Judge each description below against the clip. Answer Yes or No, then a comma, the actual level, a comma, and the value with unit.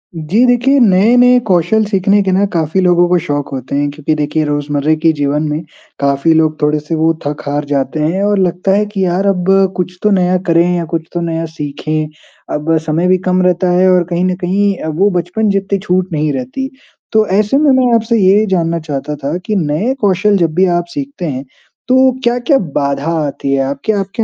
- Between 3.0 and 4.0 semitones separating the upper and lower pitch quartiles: No, average, 4.6 semitones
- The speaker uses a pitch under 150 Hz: No, medium, 175 Hz